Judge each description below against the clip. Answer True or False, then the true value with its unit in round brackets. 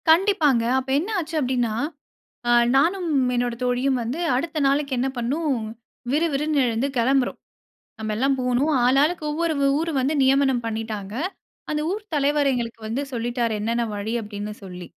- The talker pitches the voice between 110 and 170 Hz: False (265 Hz)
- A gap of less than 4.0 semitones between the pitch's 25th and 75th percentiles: False (4.3 semitones)